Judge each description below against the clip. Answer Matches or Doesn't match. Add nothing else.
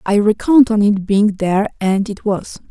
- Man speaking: Doesn't match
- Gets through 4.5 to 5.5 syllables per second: Matches